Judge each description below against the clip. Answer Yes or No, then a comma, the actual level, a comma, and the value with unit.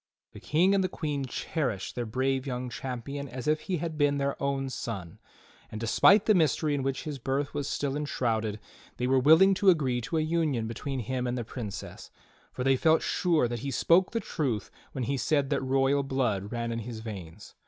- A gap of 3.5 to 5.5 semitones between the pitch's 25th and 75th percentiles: Yes, average, 4.0 semitones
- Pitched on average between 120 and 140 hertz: Yes, low, 135 Hz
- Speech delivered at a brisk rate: Yes, fast, 210 wpm